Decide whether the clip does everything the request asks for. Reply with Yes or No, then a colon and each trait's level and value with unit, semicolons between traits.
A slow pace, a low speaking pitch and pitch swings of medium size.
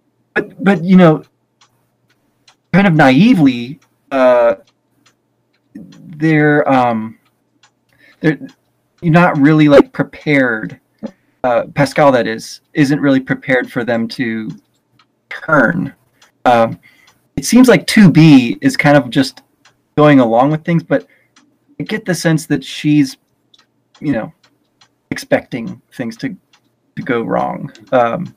No: slow, 120 wpm; medium, 145 Hz; average, 4.3 semitones